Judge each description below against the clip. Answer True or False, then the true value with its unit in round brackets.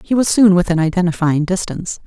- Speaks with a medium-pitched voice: True (180 Hz)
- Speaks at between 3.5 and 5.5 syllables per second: False (6.3 syllables/s)